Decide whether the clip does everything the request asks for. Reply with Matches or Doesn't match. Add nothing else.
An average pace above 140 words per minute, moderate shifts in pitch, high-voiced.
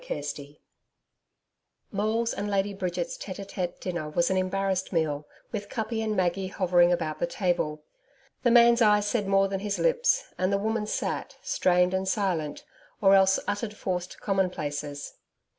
Matches